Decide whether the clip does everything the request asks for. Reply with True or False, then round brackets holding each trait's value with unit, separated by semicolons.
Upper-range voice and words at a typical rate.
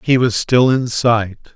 False (115 Hz; 195 wpm)